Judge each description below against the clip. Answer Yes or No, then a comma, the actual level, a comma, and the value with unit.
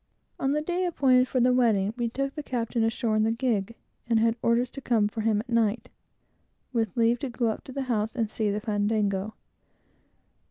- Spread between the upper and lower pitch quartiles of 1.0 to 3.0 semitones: Yes, average, 2.7 semitones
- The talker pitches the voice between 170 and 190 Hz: No, high, 230 Hz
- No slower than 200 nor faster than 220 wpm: Yes, fast, 205 wpm